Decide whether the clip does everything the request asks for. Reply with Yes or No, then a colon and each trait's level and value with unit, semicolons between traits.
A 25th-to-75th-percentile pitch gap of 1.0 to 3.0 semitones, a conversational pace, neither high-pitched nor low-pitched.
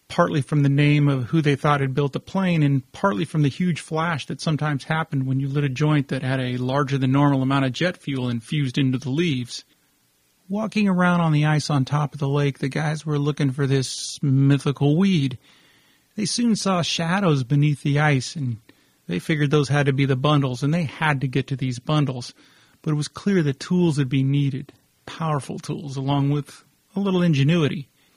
No: narrow, 2.6 semitones; fast, 210 wpm; medium, 145 Hz